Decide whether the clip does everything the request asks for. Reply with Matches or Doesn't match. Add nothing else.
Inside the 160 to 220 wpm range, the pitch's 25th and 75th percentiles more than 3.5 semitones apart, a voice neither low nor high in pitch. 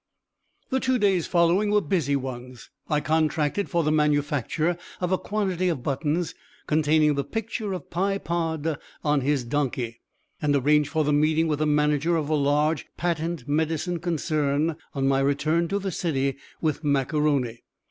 Doesn't match